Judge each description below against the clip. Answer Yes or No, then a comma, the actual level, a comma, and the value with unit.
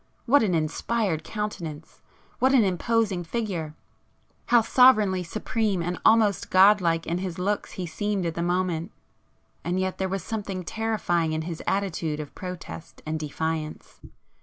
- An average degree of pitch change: Yes, average, 4.2 semitones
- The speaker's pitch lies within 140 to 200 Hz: Yes, medium, 185 Hz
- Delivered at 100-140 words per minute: Yes, slow, 135 wpm